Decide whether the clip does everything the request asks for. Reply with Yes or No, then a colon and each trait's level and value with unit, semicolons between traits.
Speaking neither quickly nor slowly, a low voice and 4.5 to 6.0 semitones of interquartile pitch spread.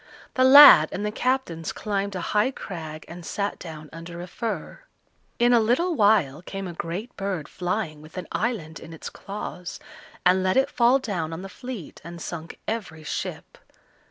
No: average, 180 wpm; high, 190 Hz; wide, 5.4 semitones